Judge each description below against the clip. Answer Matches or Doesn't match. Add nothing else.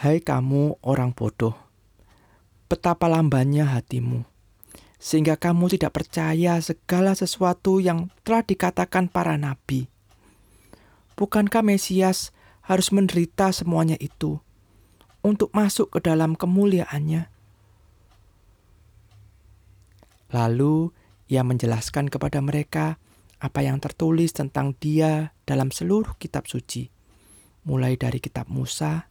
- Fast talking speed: Doesn't match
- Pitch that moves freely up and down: Matches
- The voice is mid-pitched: Matches